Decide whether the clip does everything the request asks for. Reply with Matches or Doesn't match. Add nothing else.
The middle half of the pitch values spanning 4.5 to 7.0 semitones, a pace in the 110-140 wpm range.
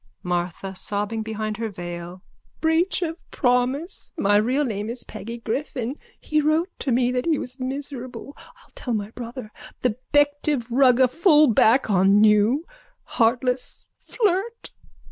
Matches